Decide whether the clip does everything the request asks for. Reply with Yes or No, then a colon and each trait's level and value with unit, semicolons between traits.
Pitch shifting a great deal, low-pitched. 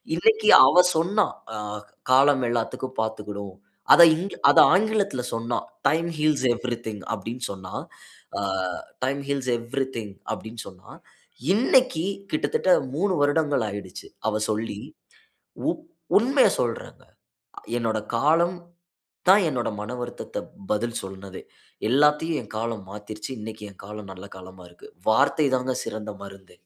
Yes: wide, 6.3 semitones; low, 120 Hz